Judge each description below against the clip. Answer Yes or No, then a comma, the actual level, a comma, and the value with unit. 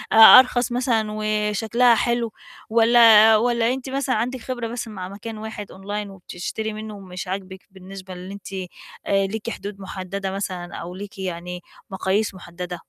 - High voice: Yes, high, 210 Hz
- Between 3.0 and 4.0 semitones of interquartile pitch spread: Yes, average, 3.3 semitones